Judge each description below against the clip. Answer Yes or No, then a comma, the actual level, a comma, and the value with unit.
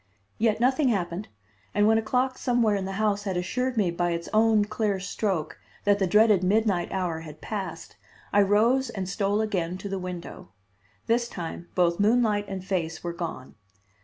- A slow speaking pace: No, average, 180 wpm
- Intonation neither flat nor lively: Yes, average, 3.6 semitones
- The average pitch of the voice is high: Yes, high, 200 Hz